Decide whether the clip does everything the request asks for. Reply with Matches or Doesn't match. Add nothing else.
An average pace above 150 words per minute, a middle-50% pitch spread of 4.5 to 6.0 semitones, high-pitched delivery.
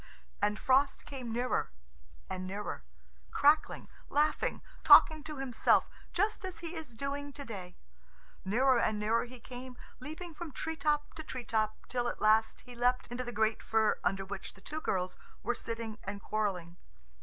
Matches